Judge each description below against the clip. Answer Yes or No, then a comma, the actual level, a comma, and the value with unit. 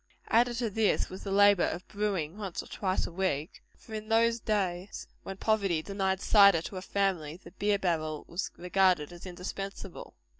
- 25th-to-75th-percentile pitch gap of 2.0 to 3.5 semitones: Yes, average, 2.8 semitones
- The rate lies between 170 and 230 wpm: Yes, average, 185 wpm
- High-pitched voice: Yes, high, 195 Hz